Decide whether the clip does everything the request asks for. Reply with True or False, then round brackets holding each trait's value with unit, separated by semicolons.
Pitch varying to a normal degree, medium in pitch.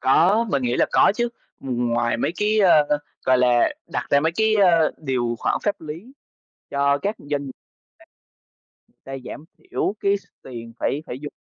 False (7.5 semitones; 145 Hz)